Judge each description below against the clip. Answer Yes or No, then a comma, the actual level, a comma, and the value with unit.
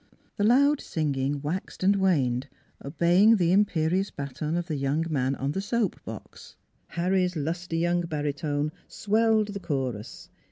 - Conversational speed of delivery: Yes, average, 145 wpm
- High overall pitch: No, medium, 170 Hz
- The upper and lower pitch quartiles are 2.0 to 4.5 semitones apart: No, average, 5.0 semitones